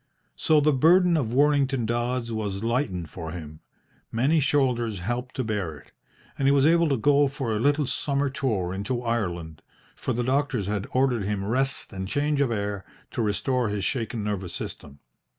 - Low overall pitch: Yes, low, 120 Hz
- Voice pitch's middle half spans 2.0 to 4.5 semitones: No, average, 5.3 semitones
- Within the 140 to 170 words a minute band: No, average, 180 wpm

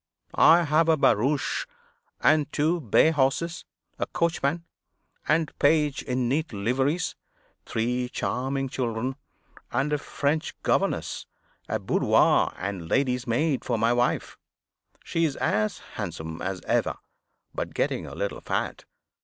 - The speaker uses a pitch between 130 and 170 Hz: Yes, low, 135 Hz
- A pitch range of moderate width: Yes, average, 4.4 semitones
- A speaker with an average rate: No, slow, 130 wpm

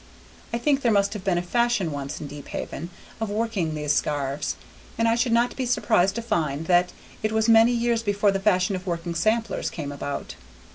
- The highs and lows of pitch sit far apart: Yes, wide, 5.7 semitones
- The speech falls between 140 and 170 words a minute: No, average, 200 wpm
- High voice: Yes, high, 200 Hz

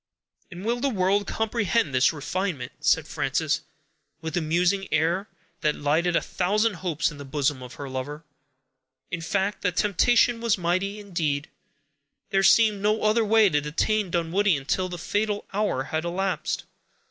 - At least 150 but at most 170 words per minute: Yes, average, 160 wpm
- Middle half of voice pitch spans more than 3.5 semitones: Yes, average, 4.8 semitones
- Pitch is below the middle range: No, medium, 185 Hz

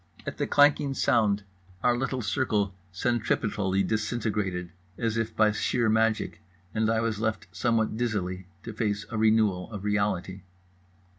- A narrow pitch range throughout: Yes, narrow, 2.2 semitones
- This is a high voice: No, low, 110 Hz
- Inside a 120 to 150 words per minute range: Yes, average, 140 wpm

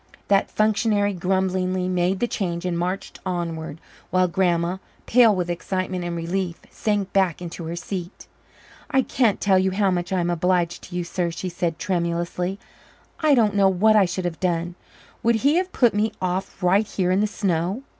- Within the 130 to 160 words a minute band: No, average, 185 wpm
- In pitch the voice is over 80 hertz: Yes, medium, 185 Hz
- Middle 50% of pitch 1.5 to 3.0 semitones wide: Yes, narrow, 2.5 semitones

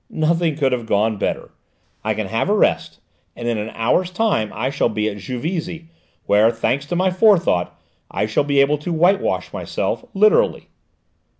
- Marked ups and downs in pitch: Yes, wide, 7.6 semitones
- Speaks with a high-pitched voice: No, medium, 140 Hz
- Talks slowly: No, average, 175 wpm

